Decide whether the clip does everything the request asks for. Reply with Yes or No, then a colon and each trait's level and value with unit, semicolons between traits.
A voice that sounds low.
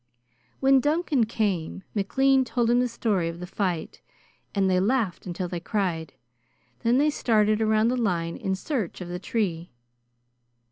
No: high, 210 Hz